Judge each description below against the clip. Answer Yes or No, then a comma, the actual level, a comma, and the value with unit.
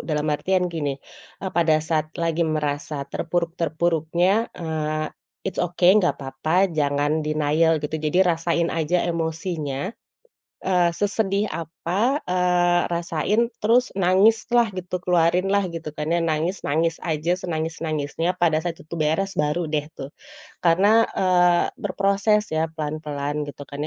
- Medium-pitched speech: Yes, medium, 165 Hz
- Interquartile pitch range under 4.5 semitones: Yes, average, 2.9 semitones